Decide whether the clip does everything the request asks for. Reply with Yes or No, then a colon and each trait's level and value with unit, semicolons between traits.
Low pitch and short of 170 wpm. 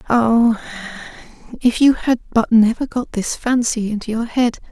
No: high, 230 Hz; average, 155 wpm